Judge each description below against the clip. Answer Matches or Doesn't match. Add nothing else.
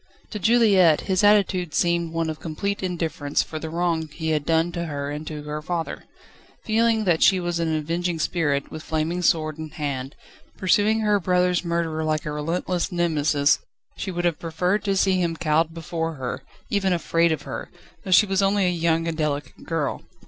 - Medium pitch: Matches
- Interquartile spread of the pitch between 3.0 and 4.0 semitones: Doesn't match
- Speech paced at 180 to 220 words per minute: Matches